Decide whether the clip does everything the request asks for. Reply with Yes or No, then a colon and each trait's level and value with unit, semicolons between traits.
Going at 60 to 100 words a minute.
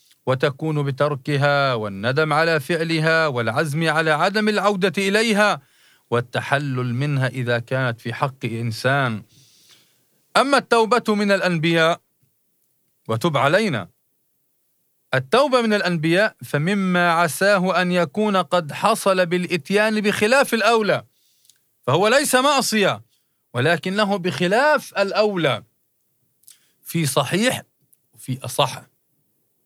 Yes: average, 90 wpm